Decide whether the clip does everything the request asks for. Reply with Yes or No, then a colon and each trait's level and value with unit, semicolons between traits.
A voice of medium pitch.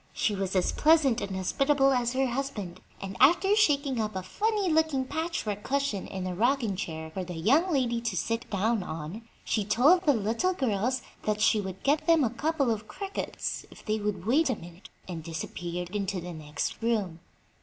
No: high, 225 Hz